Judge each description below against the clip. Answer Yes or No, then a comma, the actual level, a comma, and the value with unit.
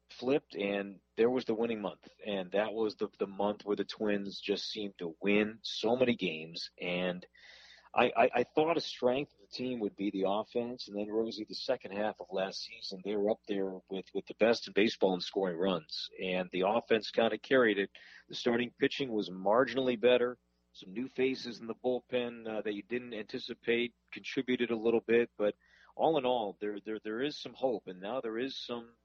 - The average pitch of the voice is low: Yes, low, 110 Hz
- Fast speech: Yes, fast, 210 wpm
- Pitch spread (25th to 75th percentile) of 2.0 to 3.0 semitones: No, average, 3.5 semitones